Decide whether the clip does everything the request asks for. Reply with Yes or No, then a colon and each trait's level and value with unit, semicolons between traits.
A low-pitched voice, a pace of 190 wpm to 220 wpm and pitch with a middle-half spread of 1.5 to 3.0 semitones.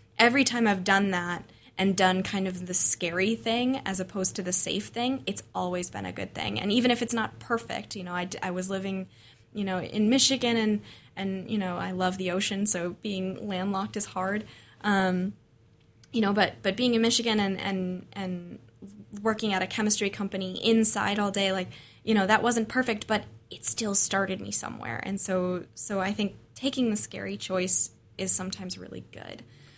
No: high, 195 Hz; average, 195 wpm; average, 2.7 semitones